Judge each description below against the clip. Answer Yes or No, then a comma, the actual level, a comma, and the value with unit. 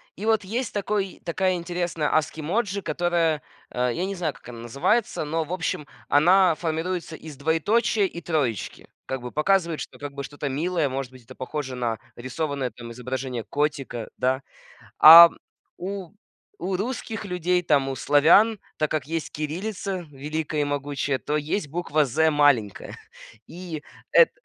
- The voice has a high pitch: No, medium, 155 Hz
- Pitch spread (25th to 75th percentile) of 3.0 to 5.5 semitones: Yes, average, 4.4 semitones